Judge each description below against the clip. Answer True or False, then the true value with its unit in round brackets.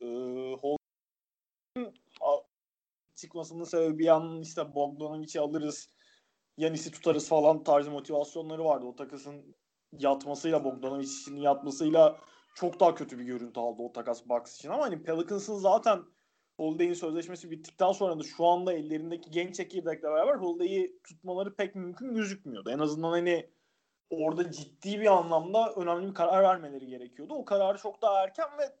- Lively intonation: False (4.1 semitones)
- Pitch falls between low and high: True (165 Hz)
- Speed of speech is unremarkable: False (145 wpm)